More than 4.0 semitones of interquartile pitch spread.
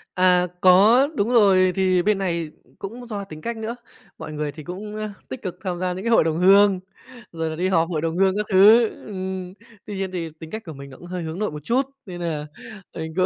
No: average, 3.7 semitones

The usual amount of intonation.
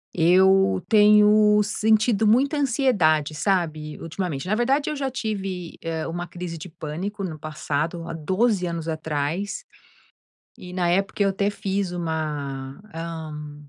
Yes: average, 4.7 semitones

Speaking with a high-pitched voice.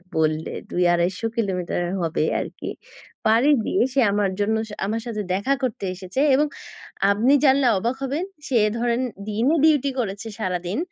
Yes: high, 215 Hz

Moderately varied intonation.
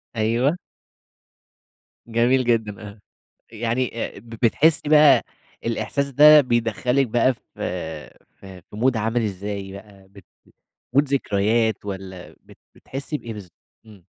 Yes: average, 3.9 semitones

